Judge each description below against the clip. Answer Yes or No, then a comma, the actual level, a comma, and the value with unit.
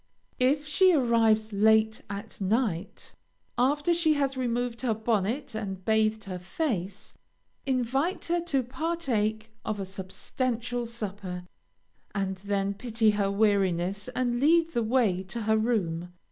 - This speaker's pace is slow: Yes, slow, 130 wpm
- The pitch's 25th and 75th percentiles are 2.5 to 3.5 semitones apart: No, average, 4.3 semitones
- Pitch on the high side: Yes, high, 220 Hz